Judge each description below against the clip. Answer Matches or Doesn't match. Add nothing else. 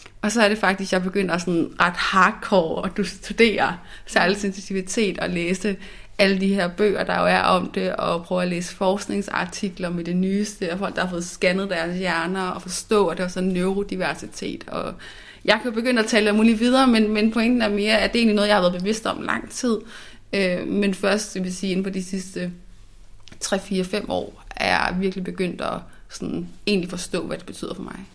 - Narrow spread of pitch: Matches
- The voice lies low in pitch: Doesn't match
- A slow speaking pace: Doesn't match